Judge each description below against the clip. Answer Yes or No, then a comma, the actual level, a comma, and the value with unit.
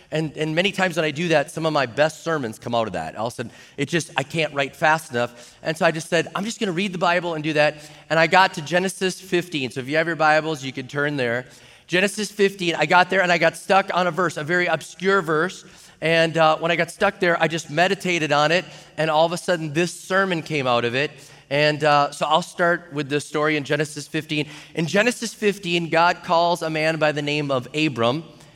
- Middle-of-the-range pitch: Yes, medium, 160 Hz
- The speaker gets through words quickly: Yes, fast, 255 wpm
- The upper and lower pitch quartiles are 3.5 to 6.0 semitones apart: No, average, 3.0 semitones